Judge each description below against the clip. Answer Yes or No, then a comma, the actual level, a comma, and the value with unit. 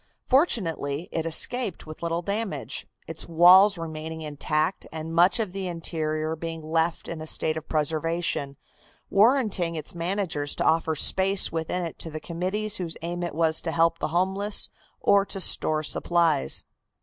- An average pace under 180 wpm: Yes, average, 160 wpm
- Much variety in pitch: No, average, 3.0 semitones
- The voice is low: No, medium, 165 Hz